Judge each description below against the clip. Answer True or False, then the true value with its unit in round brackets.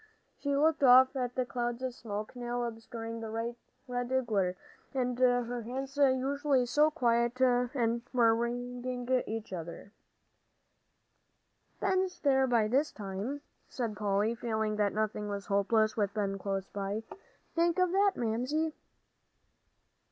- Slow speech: True (130 wpm)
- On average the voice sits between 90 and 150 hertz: False (240 Hz)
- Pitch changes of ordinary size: True (3.1 semitones)